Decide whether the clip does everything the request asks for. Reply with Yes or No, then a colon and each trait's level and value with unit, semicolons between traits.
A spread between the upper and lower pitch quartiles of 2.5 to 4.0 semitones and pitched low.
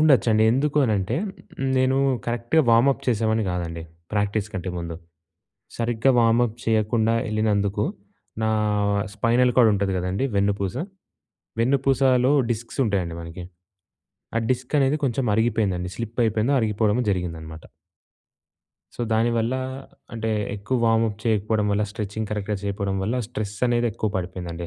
Yes: average, 3.0 semitones; low, 110 Hz